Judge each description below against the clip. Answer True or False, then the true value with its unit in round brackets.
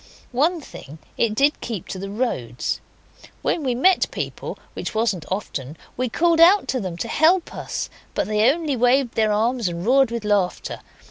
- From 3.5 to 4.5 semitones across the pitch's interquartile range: False (5.6 semitones)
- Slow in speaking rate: False (180 wpm)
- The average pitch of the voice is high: True (235 Hz)